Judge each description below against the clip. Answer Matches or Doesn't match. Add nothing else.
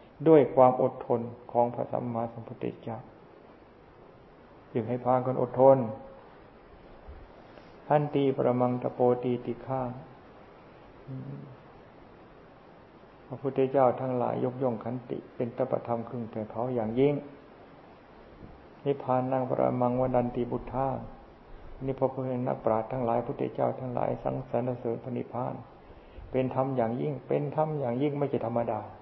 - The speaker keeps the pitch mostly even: Matches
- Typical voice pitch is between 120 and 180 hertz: Matches